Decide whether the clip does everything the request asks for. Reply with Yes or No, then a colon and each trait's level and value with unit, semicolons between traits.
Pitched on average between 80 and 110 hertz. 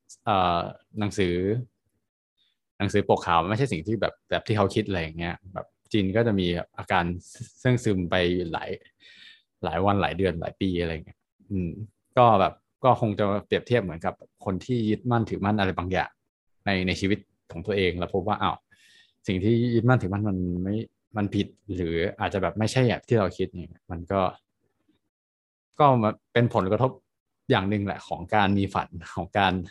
Yes: low, 100 Hz